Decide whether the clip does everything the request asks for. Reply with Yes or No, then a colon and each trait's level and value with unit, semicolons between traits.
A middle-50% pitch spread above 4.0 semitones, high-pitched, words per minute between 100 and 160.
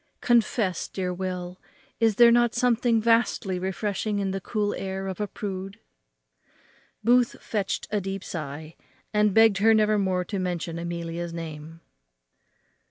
No: average, 3.4 semitones; high, 195 Hz; average, 140 wpm